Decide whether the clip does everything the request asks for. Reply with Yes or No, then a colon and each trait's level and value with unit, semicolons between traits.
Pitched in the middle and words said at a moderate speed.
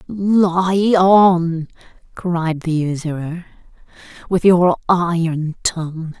No: medium, 175 Hz; slow, 85 wpm